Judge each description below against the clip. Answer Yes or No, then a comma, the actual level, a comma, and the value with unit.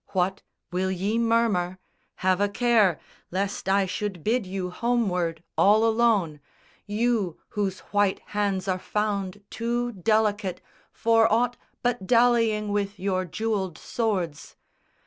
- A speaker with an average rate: No, slow, 125 wpm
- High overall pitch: Yes, high, 205 Hz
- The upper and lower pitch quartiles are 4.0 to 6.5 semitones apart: No, average, 3.3 semitones